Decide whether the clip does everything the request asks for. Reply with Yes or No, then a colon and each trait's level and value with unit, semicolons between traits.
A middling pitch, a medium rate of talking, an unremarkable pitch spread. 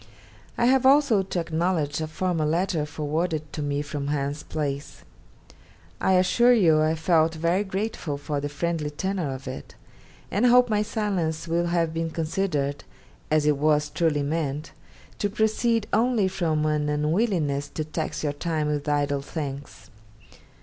Yes: medium, 160 Hz; average, 155 wpm; average, 4.2 semitones